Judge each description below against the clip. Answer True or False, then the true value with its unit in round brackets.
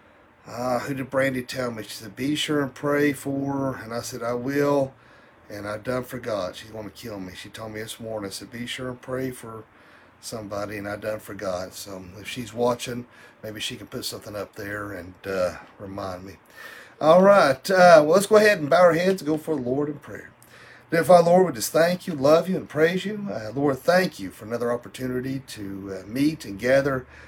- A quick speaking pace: True (225 wpm)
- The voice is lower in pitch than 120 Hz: False (125 Hz)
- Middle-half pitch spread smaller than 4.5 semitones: False (5.4 semitones)